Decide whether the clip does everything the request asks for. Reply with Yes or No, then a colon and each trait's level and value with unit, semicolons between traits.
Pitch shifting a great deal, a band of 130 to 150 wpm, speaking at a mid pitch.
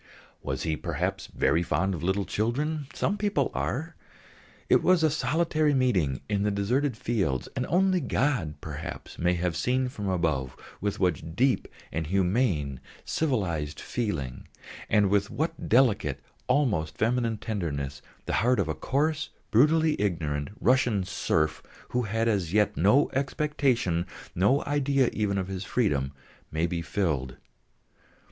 No: wide, 7.8 semitones; average, 140 wpm; low, 105 Hz